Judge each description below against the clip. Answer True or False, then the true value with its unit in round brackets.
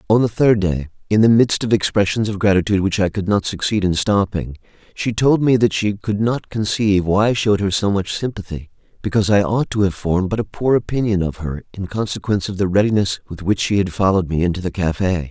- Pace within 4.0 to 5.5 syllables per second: False (6.0 syllables/s)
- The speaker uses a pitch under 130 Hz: True (100 Hz)